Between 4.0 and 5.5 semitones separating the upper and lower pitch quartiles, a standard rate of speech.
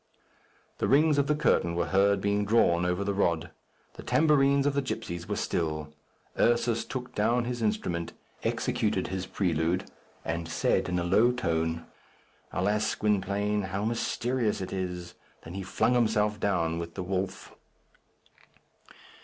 Yes: average, 5.1 semitones; average, 145 wpm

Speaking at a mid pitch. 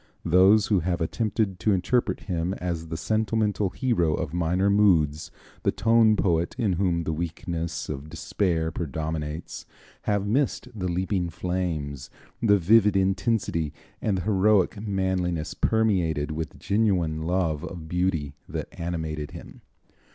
No: very low, 90 Hz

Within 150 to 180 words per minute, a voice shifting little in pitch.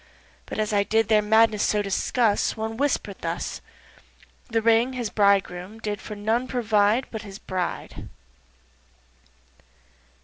No: slow, 135 wpm; narrow, 1.8 semitones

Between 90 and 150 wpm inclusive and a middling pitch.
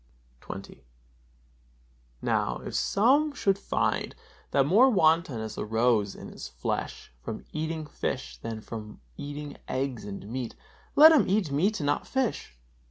Yes: average, 140 wpm; medium, 145 Hz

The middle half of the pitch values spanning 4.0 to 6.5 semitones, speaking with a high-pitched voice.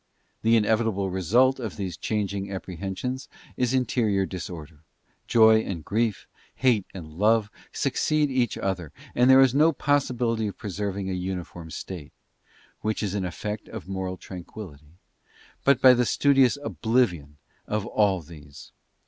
No: average, 4.6 semitones; low, 105 Hz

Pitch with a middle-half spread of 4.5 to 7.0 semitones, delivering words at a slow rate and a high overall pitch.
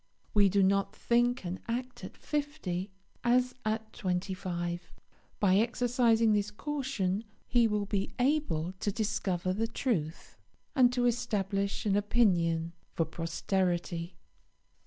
Yes: average, 4.8 semitones; slow, 125 wpm; high, 205 Hz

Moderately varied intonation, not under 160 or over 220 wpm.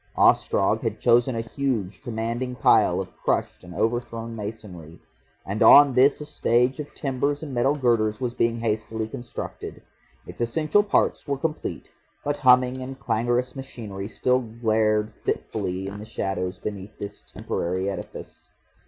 No: average, 3.3 semitones; average, 145 wpm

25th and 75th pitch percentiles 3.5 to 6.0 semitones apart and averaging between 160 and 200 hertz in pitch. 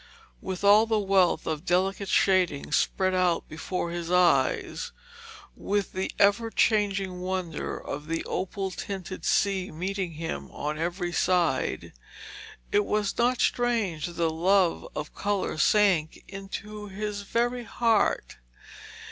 No: average, 2.9 semitones; high, 190 Hz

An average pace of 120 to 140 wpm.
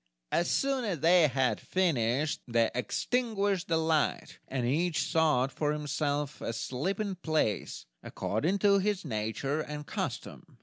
Yes: slow, 135 wpm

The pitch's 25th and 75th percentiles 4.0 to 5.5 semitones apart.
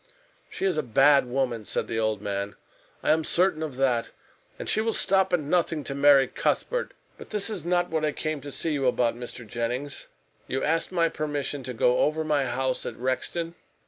Yes: average, 4.6 semitones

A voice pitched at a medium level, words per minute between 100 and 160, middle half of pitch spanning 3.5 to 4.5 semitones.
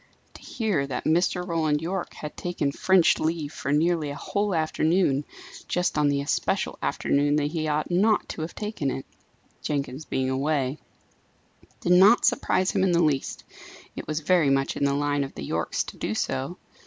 No: medium, 155 Hz; average, 180 wpm; average, 3.9 semitones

